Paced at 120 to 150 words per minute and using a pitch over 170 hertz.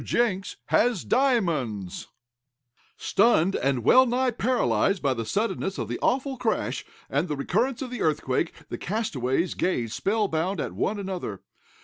Yes: average, 145 wpm; high, 190 Hz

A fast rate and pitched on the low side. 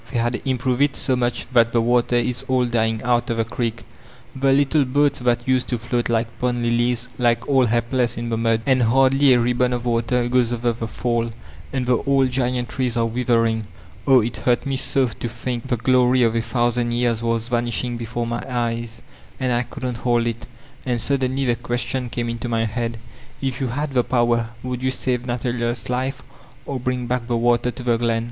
Yes: fast, 210 wpm; low, 120 Hz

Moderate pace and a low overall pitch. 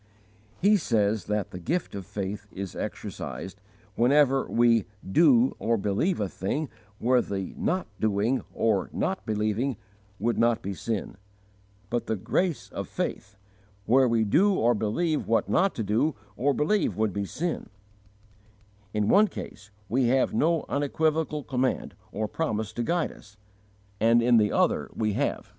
Yes: average, 150 wpm; low, 115 Hz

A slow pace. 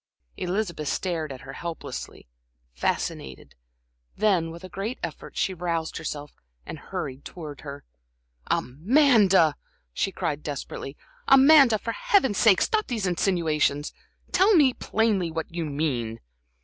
Yes: slow, 125 wpm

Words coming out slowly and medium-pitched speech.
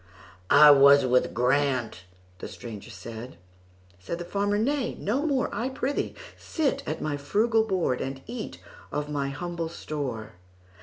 Yes: slow, 120 wpm; medium, 145 Hz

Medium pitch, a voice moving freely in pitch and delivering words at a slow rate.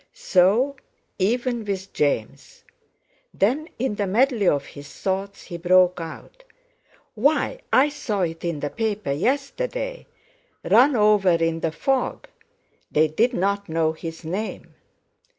No: high, 200 Hz; wide, 7.1 semitones; slow, 125 wpm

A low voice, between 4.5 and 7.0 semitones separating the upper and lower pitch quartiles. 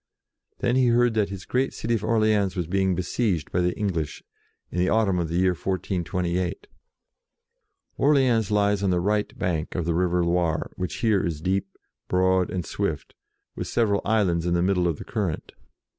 No: very low, 95 Hz; average, 3.3 semitones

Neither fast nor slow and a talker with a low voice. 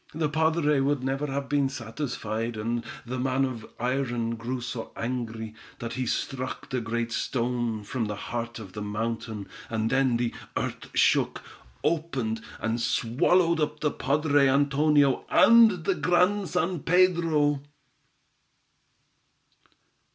No: slow, 130 wpm; low, 130 Hz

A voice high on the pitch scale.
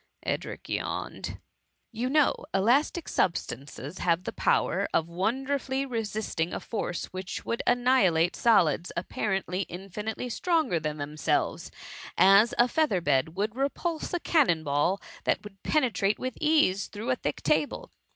Yes: high, 200 Hz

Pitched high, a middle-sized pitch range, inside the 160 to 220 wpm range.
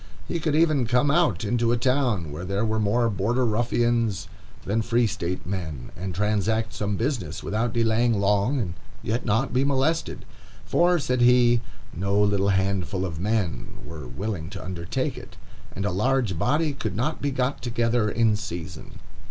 No: low, 110 Hz; average, 3.9 semitones; average, 170 wpm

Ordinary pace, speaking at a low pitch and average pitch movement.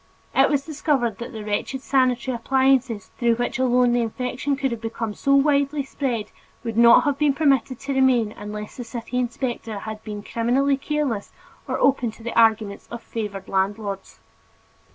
No: average, 175 wpm; high, 240 Hz; average, 3.3 semitones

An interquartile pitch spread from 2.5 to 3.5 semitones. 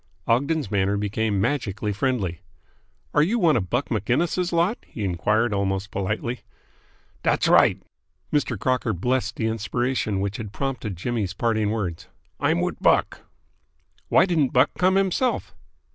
No: average, 5.3 semitones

